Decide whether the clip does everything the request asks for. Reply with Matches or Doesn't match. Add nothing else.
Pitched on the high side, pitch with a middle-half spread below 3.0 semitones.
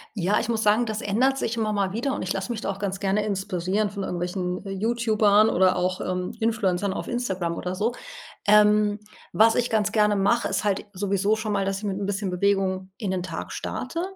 Matches